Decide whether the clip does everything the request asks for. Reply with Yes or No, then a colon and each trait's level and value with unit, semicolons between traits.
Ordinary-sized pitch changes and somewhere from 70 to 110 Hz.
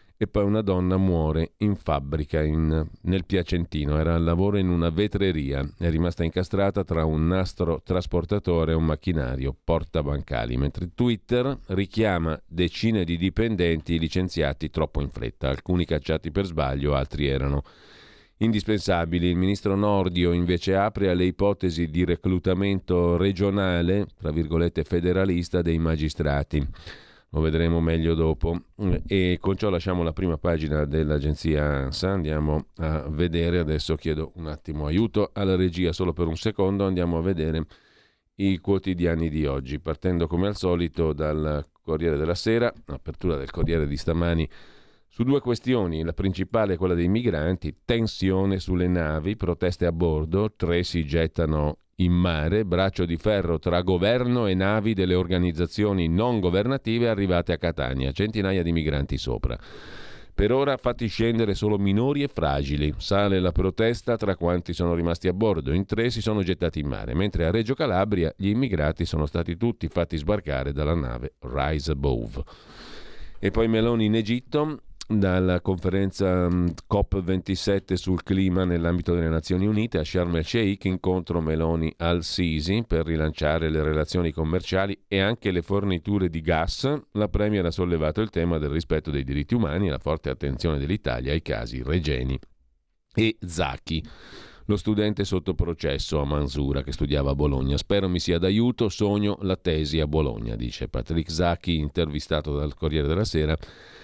Yes: average, 3.8 semitones; very low, 85 Hz